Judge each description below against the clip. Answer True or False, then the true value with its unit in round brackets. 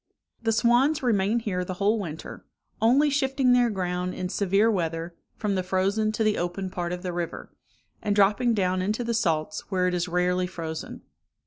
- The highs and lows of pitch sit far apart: False (3.9 semitones)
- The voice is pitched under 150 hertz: False (195 Hz)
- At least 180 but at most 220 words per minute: True (185 wpm)